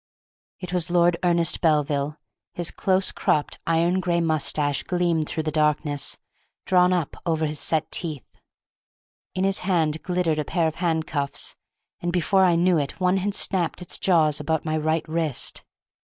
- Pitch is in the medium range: Yes, medium, 165 Hz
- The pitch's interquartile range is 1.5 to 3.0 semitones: Yes, narrow, 2.6 semitones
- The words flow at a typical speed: Yes, average, 160 wpm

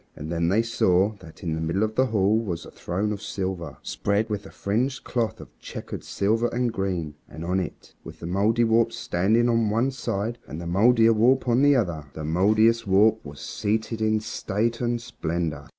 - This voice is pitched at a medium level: No, low, 105 Hz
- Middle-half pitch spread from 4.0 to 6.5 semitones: Yes, average, 4.7 semitones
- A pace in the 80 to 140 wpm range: No, average, 190 wpm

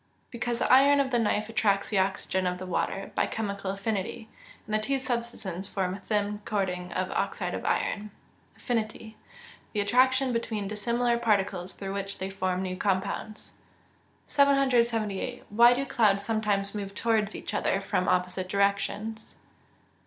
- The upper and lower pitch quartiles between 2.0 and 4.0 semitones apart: Yes, average, 3.2 semitones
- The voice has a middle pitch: No, high, 210 Hz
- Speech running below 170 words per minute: Yes, average, 150 wpm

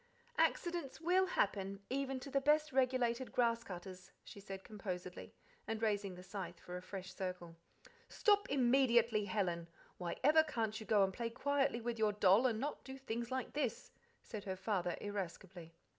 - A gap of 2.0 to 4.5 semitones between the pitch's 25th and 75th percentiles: No, wide, 5.6 semitones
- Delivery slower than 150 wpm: No, average, 170 wpm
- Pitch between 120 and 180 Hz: No, high, 220 Hz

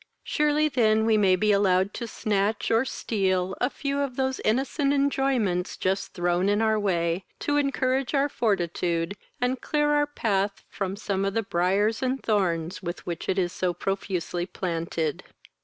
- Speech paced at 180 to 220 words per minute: No, average, 165 wpm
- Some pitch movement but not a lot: No, wide, 5.9 semitones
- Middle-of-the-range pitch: No, high, 205 Hz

